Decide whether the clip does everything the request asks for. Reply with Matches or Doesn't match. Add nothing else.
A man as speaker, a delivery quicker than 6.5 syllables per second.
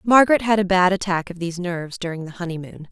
Doesn't match